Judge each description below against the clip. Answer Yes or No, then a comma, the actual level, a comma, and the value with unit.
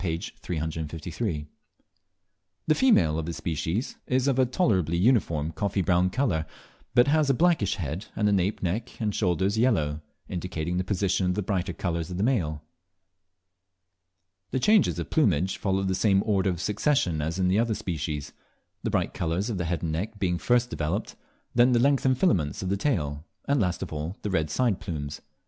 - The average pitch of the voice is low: Yes, very low, 95 Hz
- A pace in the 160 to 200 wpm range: Yes, average, 180 wpm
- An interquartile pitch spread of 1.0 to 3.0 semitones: No, wide, 5.5 semitones